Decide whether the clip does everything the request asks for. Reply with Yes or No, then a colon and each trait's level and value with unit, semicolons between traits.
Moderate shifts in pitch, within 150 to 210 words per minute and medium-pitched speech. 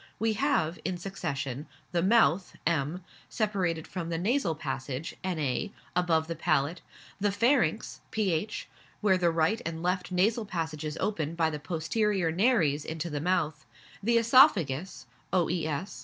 No: average, 4.3 semitones; average, 140 wpm; medium, 170 Hz